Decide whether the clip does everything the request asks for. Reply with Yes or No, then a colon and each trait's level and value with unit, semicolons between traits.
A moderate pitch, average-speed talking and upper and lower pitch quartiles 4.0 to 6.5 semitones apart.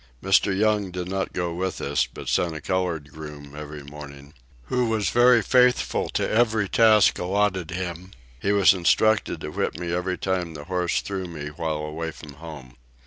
No: very low, 90 Hz; average, 180 wpm; average, 4.4 semitones